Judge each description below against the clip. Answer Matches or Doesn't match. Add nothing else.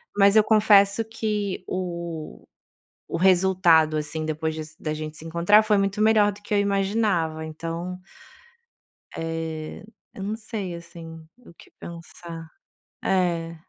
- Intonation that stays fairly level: Doesn't match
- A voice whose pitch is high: Doesn't match